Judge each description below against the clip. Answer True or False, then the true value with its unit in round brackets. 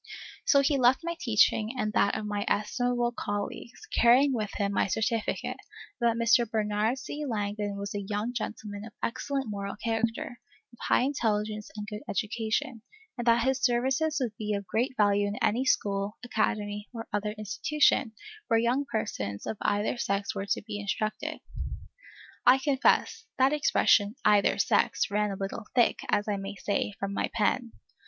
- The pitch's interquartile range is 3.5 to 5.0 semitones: False (3.1 semitones)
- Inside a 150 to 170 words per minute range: True (165 wpm)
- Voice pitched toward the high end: True (220 Hz)